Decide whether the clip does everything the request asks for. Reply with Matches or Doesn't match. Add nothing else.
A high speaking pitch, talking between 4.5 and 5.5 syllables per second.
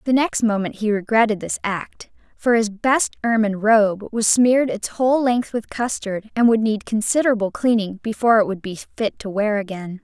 Matches